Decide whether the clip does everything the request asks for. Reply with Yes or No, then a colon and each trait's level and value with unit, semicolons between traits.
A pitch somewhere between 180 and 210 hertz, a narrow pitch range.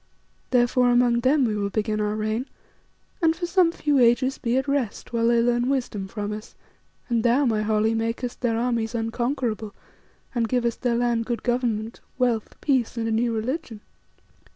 No: high, 235 Hz; narrow, 2.1 semitones